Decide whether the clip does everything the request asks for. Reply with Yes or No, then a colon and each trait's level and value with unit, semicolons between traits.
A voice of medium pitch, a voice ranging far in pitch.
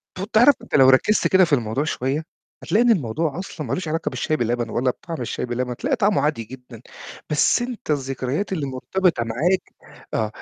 Yes: medium, 150 Hz; wide, 6.9 semitones